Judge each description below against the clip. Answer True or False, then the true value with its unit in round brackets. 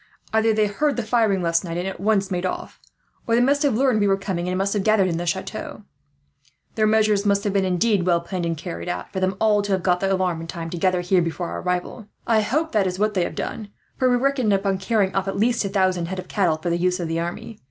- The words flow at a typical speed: False (275 wpm)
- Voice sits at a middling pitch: False (195 Hz)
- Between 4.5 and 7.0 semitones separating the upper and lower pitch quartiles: False (3.3 semitones)